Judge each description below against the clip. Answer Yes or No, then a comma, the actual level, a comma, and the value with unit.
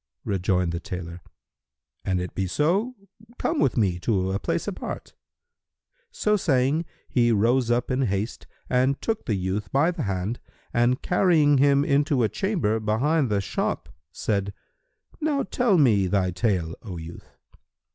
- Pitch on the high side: No, low, 115 Hz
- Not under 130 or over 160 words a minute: Yes, average, 150 wpm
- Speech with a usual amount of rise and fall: No, wide, 7.2 semitones